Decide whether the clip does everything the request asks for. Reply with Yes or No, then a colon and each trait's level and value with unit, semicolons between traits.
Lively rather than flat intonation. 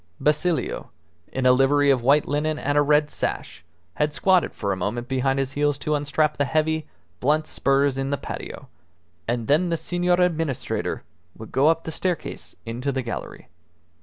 No: average, 2.7 semitones